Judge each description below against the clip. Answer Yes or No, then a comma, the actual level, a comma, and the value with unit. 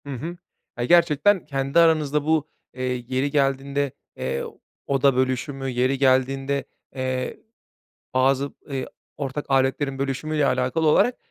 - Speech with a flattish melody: Yes, narrow, 2.3 semitones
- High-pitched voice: No, low, 135 Hz